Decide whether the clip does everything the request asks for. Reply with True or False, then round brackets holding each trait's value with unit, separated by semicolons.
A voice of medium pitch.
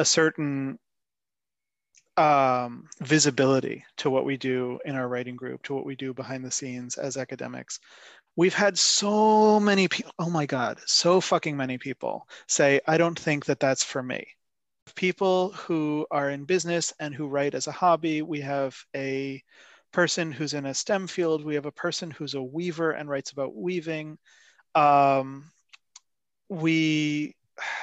True (150 Hz)